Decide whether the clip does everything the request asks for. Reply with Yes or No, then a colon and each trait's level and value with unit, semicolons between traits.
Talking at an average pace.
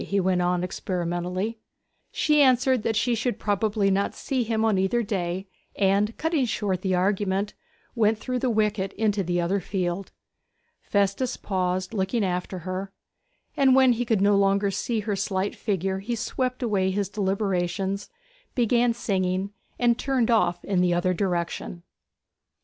Yes: average, 155 wpm